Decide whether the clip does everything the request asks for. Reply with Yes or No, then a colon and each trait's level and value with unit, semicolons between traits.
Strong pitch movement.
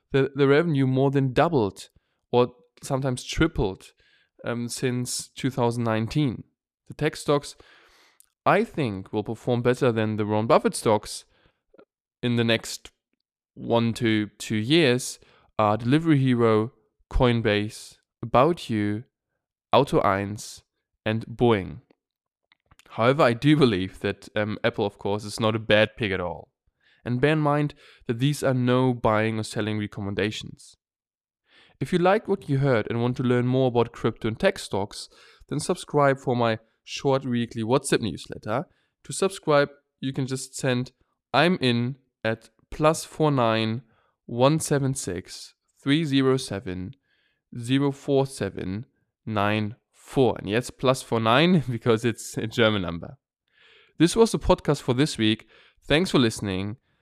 No: average, 4.3 semitones